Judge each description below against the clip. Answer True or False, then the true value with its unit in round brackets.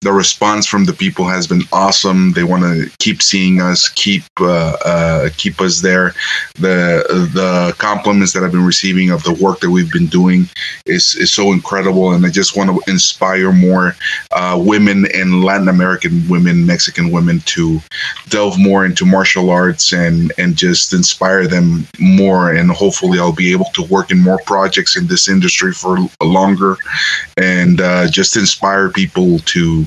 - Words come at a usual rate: True (175 wpm)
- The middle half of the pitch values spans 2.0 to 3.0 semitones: True (2.7 semitones)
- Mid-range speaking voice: False (95 Hz)